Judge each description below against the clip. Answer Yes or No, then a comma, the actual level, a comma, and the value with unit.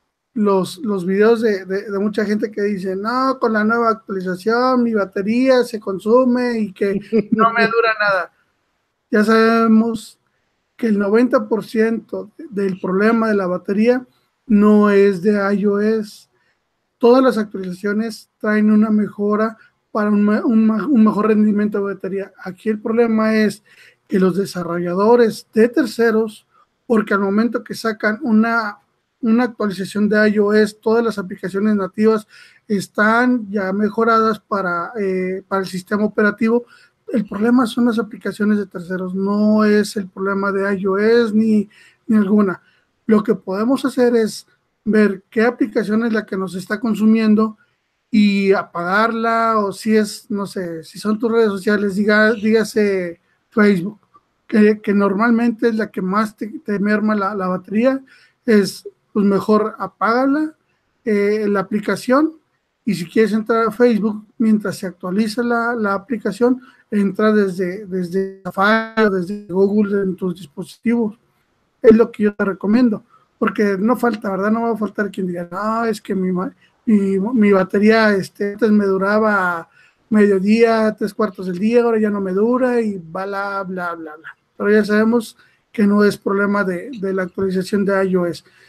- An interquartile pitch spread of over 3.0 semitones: No, narrow, 2.4 semitones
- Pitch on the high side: Yes, high, 215 Hz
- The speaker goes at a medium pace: Yes, average, 155 wpm